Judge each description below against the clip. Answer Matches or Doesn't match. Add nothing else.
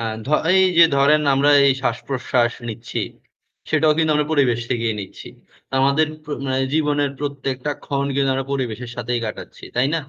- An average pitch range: Matches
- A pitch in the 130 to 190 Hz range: Matches